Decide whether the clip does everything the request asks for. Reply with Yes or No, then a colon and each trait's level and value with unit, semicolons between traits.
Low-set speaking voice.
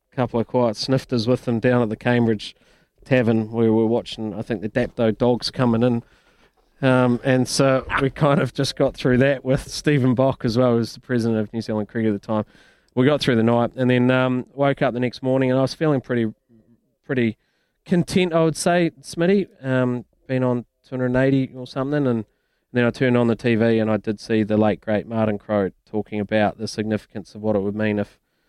Yes: low, 125 Hz